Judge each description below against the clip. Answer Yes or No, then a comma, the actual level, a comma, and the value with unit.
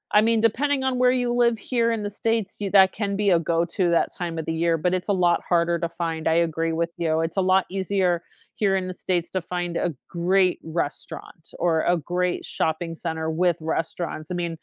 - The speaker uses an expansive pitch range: No, average, 3.0 semitones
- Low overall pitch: No, medium, 175 Hz